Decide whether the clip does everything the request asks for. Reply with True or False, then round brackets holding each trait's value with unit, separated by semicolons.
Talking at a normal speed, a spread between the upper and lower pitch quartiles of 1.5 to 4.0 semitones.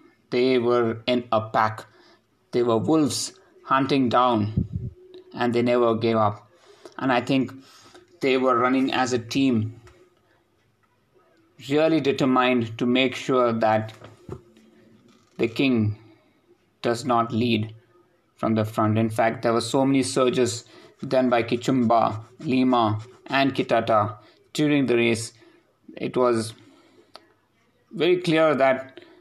False (120 wpm; 2.7 semitones)